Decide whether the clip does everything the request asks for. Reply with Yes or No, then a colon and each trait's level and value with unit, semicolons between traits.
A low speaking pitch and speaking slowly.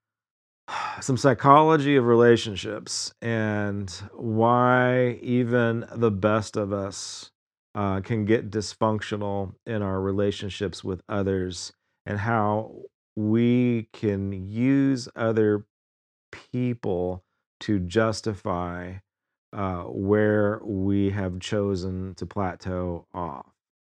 Yes: low, 105 Hz; slow, 95 wpm